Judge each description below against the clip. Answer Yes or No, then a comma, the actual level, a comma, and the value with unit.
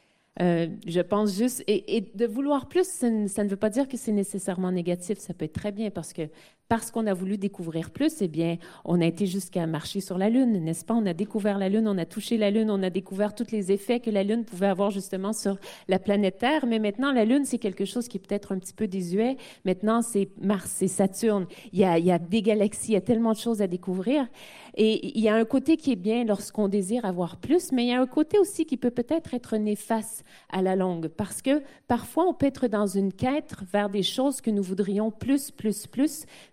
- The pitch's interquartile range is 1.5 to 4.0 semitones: Yes, average, 3.6 semitones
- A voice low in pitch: No, high, 210 Hz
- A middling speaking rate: No, fast, 250 wpm